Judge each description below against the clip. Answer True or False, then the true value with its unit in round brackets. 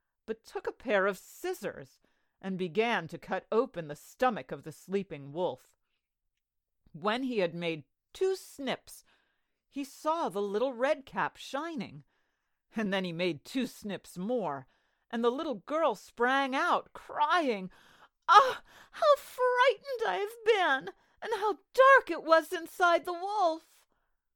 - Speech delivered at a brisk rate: False (145 wpm)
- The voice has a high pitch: True (260 Hz)